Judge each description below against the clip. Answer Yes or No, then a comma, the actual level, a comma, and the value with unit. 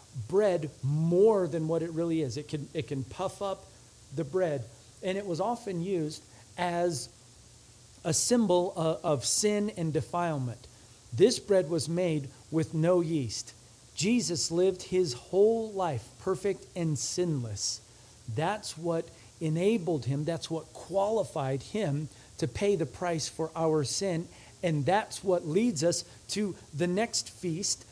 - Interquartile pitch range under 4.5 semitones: No, average, 5.1 semitones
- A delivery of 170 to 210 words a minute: No, average, 145 wpm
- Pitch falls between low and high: Yes, medium, 165 Hz